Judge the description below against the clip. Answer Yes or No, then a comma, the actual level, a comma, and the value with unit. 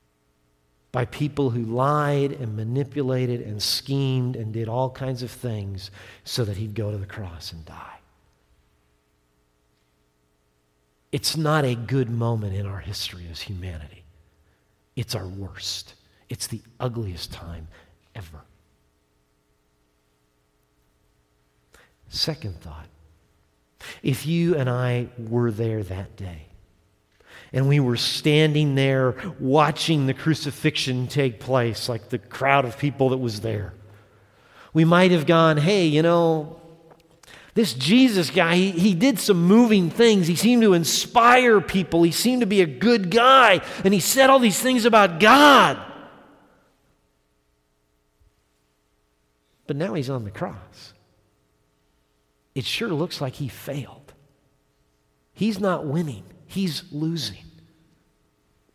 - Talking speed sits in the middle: No, slow, 125 wpm